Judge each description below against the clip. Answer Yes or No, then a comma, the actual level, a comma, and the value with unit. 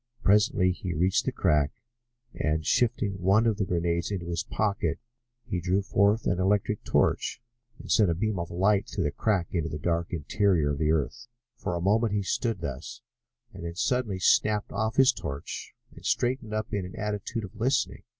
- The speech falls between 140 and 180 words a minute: No, average, 190 wpm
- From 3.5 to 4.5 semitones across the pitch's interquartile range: Yes, average, 4.0 semitones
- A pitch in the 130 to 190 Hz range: No, very low, 95 Hz